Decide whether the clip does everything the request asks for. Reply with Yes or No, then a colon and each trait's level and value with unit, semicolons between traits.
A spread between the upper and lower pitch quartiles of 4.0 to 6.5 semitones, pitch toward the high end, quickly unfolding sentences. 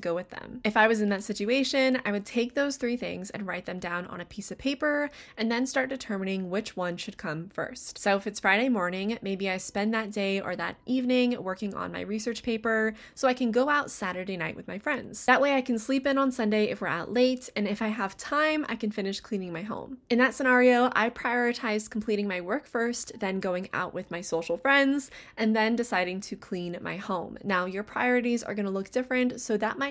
Yes: average, 4.6 semitones; high, 220 Hz; fast, 235 wpm